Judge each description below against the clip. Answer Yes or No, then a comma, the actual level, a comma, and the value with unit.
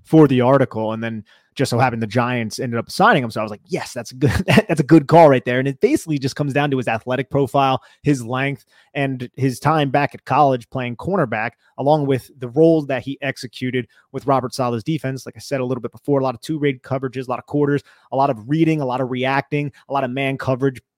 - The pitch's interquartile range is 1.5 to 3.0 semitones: Yes, narrow, 2.5 semitones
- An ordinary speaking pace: No, fast, 255 wpm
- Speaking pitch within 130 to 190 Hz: Yes, low, 135 Hz